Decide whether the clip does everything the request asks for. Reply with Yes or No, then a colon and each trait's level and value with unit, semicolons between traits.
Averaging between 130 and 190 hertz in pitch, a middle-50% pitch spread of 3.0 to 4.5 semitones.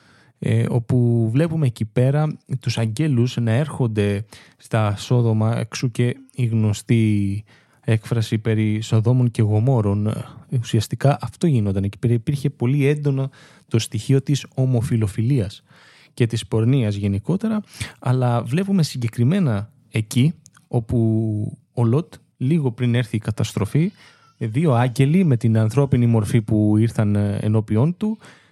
No: low, 120 Hz; average, 4.0 semitones